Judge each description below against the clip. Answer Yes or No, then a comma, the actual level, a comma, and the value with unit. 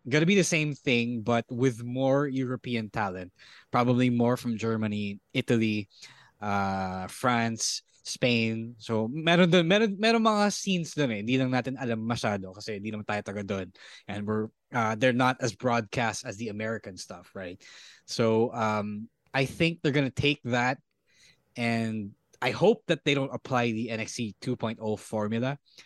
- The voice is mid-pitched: No, low, 120 Hz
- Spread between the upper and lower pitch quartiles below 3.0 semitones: No, average, 3.5 semitones